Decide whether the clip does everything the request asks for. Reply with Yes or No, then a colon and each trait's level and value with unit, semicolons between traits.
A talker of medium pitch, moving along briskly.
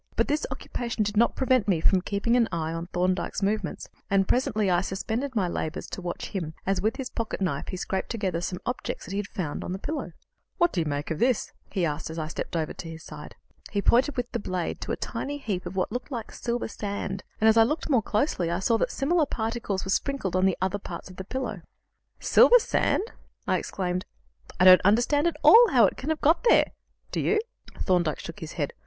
No: high, 200 Hz; fast, 230 wpm